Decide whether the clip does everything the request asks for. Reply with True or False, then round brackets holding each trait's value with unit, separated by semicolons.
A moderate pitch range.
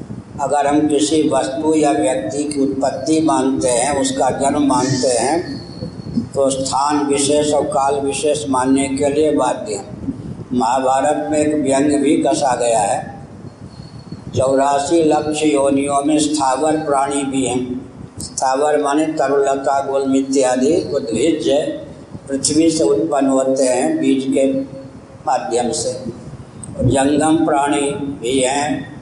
False (1.8 semitones)